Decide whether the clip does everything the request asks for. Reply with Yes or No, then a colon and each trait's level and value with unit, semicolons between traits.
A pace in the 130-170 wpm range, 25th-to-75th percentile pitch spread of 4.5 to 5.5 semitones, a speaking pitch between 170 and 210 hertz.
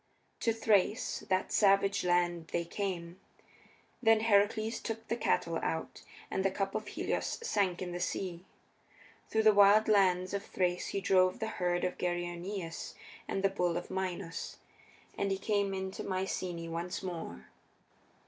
No: average, 150 wpm; narrow, 2.4 semitones; high, 190 Hz